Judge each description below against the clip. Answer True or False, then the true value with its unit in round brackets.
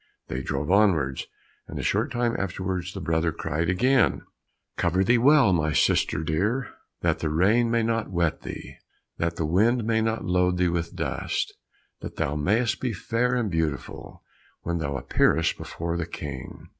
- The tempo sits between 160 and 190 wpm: True (170 wpm)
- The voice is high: False (90 Hz)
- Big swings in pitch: True (5.7 semitones)